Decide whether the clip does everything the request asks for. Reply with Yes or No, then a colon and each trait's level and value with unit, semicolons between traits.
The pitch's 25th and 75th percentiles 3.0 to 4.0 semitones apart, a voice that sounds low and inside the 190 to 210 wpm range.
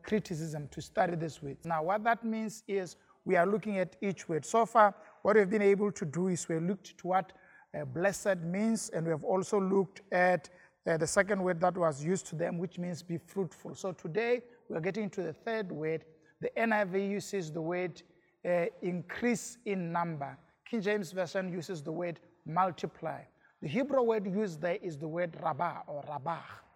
No: average, 3.4 semitones; medium, 185 Hz; average, 195 wpm